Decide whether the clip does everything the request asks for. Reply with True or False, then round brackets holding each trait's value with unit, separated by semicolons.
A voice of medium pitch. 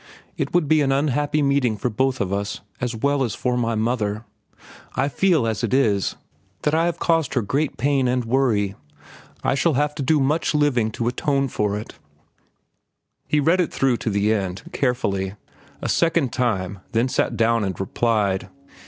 False (125 Hz)